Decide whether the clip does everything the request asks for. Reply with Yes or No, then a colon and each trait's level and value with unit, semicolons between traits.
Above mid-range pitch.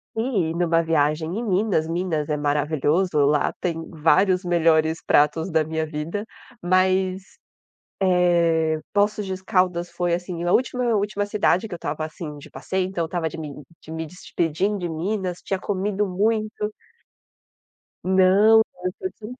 No: medium, 175 Hz